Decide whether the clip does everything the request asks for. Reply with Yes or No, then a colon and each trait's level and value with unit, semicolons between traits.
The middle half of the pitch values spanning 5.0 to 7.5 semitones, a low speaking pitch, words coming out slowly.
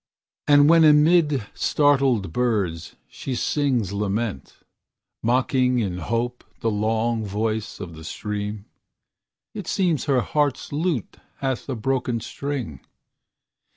Yes: average, 5.3 semitones; low, 120 Hz; slow, 115 wpm